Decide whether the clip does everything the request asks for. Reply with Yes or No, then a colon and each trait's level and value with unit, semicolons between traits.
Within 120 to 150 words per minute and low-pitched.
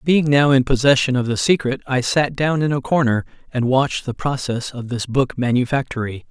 No: average, 200 wpm; low, 130 Hz